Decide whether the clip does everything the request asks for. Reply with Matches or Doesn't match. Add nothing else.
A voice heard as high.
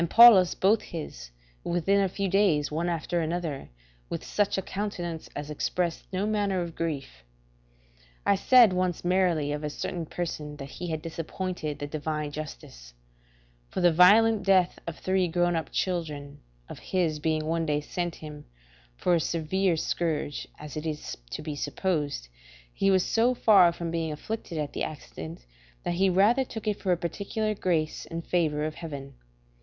Doesn't match